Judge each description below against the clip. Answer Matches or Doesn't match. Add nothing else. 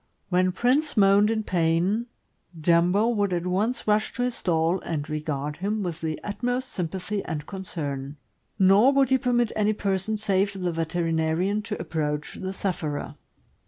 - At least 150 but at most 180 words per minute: Matches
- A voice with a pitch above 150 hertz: Matches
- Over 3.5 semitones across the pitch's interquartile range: Matches